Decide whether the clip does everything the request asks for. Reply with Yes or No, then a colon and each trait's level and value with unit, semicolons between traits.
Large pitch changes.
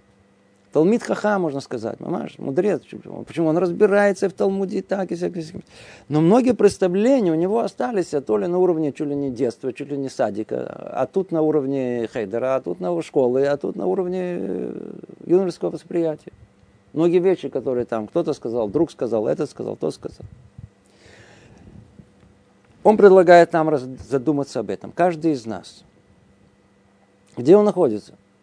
Yes: wide, 8.9 semitones